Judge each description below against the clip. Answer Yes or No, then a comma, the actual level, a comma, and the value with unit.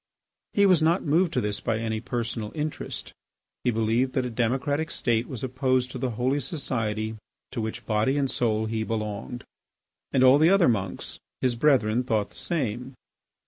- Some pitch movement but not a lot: Yes, average, 3.7 semitones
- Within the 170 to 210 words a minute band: Yes, average, 175 wpm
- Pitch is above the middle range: No, low, 125 Hz